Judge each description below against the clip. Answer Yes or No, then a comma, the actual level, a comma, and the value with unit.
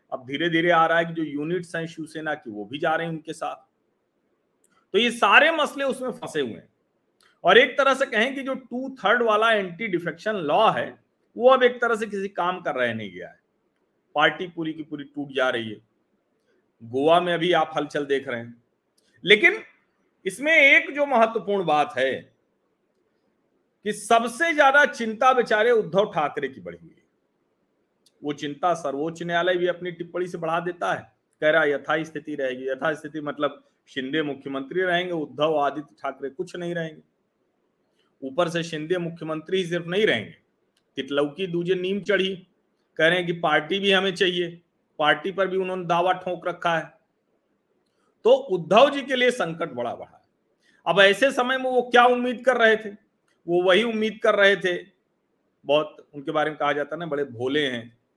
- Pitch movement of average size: No, wide, 5.9 semitones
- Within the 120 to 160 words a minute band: No, average, 180 wpm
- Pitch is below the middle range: No, medium, 175 Hz